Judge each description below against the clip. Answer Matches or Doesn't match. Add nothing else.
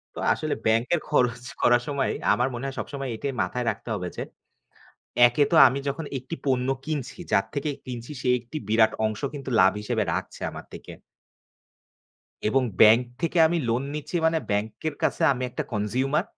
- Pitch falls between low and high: Doesn't match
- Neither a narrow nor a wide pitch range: Matches